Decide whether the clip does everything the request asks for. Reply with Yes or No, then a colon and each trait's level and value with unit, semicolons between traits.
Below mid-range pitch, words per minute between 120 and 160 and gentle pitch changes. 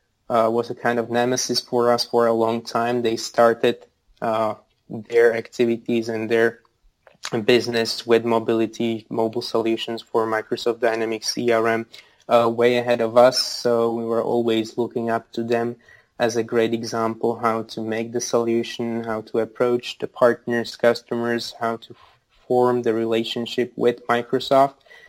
Yes: low, 115 Hz; average, 155 wpm; narrow, 0.9 semitones